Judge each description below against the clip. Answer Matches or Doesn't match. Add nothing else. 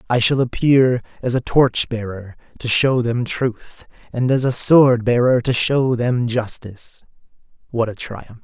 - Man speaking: Matches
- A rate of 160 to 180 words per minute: Matches